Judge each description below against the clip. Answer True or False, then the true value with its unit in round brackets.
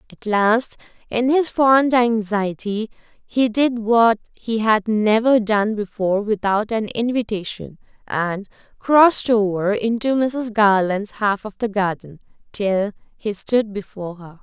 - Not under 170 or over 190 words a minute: False (135 wpm)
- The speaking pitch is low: False (220 Hz)